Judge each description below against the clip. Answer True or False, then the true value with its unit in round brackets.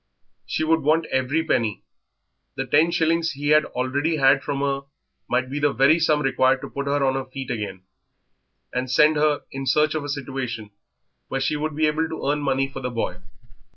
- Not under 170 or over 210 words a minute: True (200 wpm)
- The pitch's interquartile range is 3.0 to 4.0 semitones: False (2.6 semitones)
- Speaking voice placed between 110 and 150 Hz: True (140 Hz)